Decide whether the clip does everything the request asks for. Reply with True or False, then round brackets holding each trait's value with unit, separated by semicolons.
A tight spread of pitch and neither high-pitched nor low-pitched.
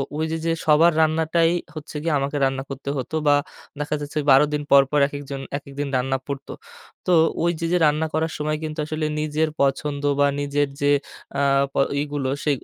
True (1.9 semitones; 145 Hz)